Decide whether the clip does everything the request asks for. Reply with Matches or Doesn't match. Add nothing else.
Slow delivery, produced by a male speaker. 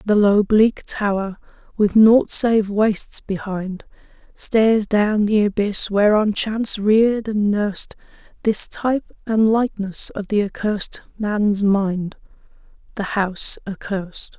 Doesn't match